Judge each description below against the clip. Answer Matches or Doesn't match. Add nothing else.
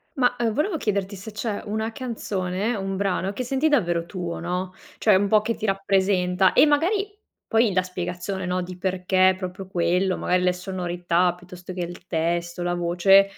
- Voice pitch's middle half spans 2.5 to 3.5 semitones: Matches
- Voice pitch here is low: Doesn't match